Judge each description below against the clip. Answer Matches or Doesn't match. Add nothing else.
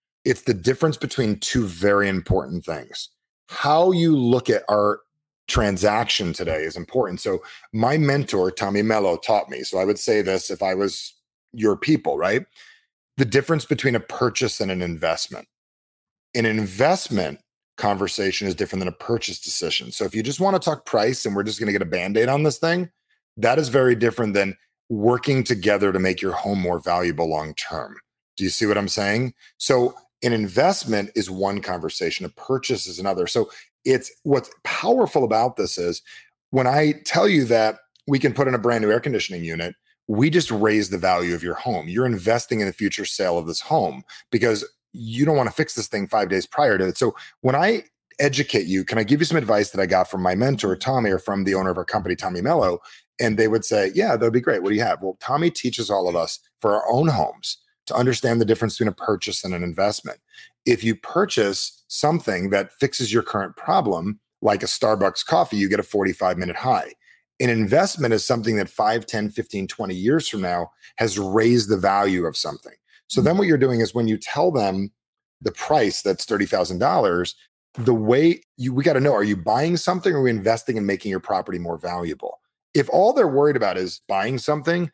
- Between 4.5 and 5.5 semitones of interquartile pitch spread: Matches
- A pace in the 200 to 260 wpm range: Matches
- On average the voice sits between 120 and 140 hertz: Doesn't match